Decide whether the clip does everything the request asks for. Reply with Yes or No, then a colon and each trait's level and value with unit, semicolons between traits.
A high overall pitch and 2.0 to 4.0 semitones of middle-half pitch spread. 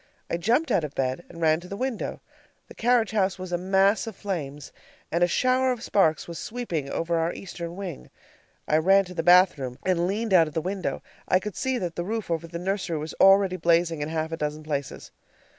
No: medium, 175 Hz; average, 3.5 semitones